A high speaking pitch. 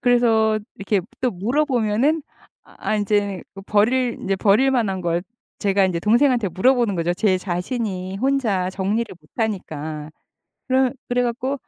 Yes: high, 210 Hz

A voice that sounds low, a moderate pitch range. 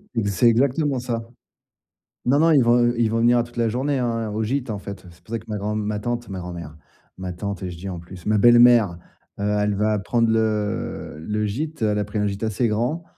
Yes: low, 110 Hz; average, 3.0 semitones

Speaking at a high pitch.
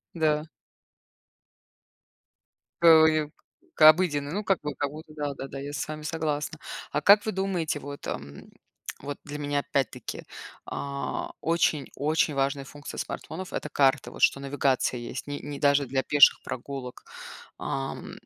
No: medium, 145 Hz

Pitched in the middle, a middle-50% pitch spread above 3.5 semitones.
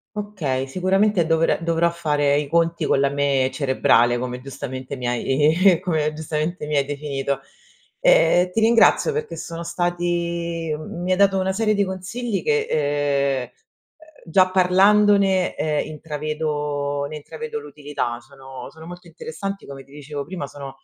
Yes: medium, 160 Hz; average, 4.7 semitones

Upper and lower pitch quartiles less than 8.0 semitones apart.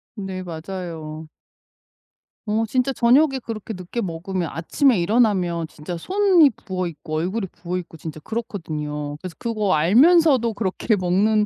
Yes: wide, 5.5 semitones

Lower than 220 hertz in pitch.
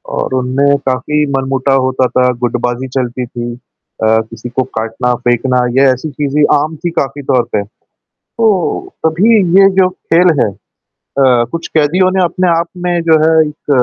Yes: medium, 140 Hz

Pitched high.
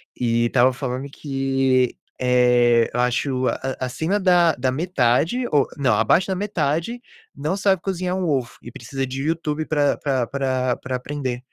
No: low, 135 Hz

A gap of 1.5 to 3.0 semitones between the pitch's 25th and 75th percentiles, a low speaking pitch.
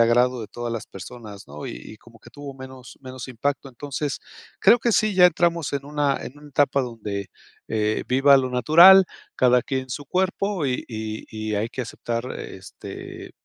No: average, 3.8 semitones; low, 130 Hz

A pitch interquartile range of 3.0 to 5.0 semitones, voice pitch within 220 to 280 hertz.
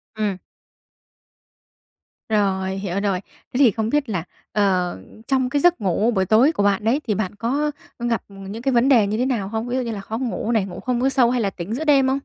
Yes: average, 4.4 semitones; high, 225 Hz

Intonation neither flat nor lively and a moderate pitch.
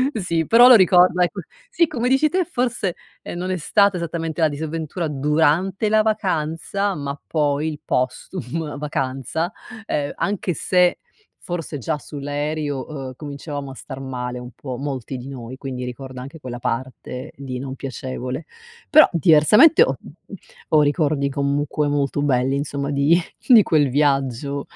Yes: average, 4.3 semitones; medium, 150 Hz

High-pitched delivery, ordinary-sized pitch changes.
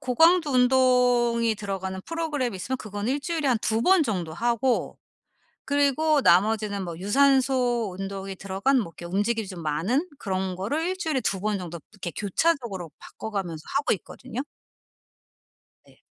No: high, 230 Hz; wide, 5.9 semitones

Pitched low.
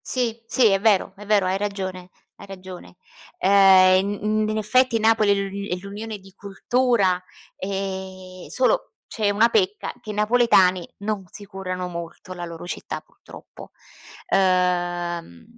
No: high, 195 Hz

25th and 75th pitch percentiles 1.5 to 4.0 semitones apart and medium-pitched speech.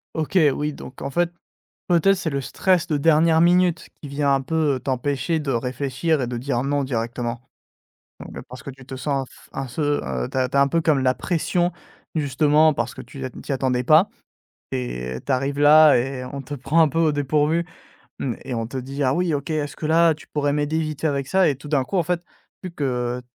Yes: average, 3.5 semitones; medium, 145 Hz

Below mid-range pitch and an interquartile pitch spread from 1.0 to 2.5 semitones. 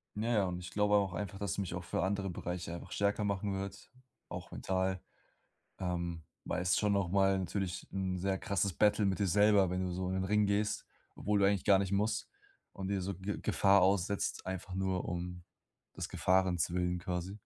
Yes: very low, 95 Hz; narrow, 1.9 semitones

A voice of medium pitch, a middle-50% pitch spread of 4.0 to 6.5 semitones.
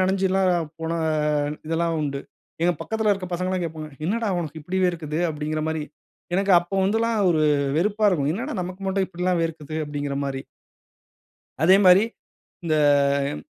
No: medium, 175 Hz; average, 3.4 semitones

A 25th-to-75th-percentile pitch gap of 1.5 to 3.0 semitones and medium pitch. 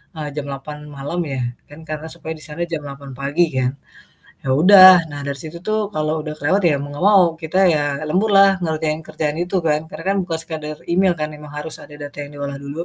Yes: narrow, 2.5 semitones; medium, 155 Hz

